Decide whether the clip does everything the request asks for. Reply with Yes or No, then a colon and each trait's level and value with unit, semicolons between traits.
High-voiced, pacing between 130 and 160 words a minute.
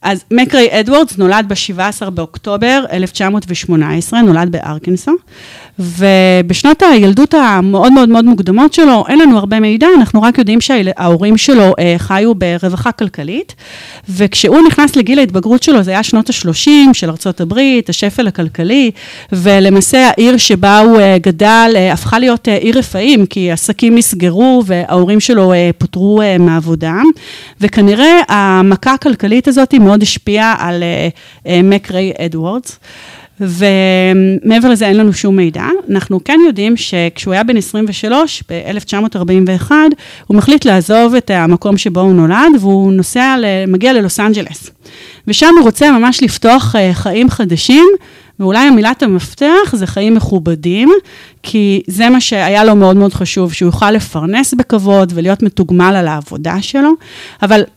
Yes: high, 205 Hz; average, 135 wpm